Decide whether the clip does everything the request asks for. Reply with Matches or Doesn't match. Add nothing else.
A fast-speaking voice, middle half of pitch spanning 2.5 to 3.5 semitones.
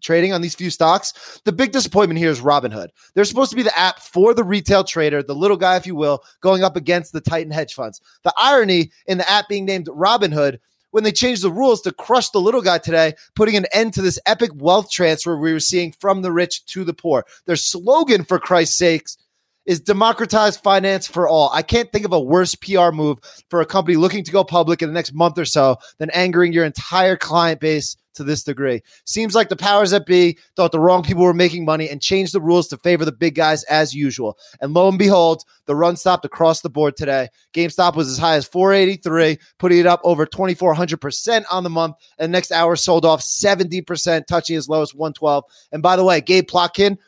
Matches